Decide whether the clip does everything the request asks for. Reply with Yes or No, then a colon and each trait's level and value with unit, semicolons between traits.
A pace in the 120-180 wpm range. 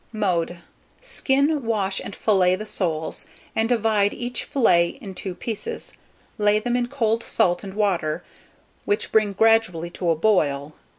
Yes: average, 150 wpm